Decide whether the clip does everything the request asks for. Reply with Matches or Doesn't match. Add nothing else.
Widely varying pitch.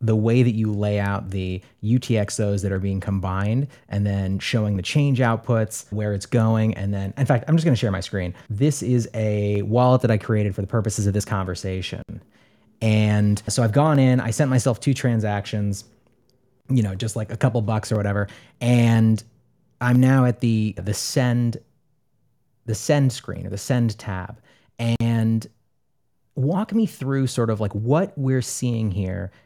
Doesn't match